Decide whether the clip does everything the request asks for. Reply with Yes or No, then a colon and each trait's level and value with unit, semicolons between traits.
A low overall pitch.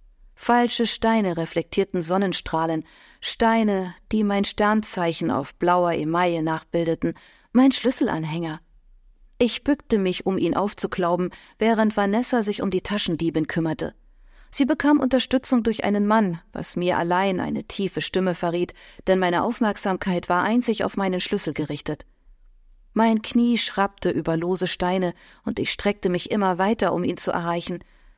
No: high, 190 Hz